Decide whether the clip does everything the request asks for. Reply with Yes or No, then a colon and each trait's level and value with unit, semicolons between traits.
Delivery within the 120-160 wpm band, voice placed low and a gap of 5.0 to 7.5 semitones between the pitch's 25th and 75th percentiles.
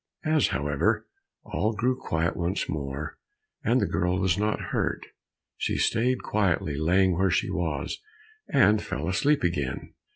Yes: average, 140 wpm; very low, 90 Hz; average, 5.3 semitones